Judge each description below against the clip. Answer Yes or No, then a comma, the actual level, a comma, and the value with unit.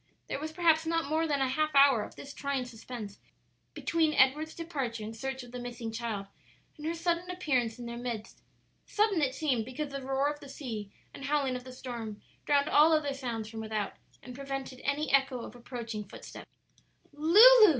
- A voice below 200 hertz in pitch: No, very high, 270 Hz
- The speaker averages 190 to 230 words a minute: Yes, average, 195 wpm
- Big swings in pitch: No, average, 4.3 semitones